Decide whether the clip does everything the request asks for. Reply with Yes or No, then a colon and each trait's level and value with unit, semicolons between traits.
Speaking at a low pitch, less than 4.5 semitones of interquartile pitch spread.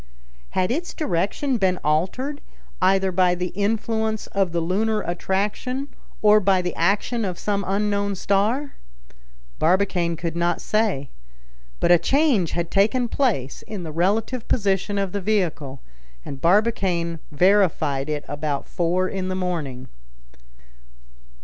No: high, 190 Hz; average, 3.8 semitones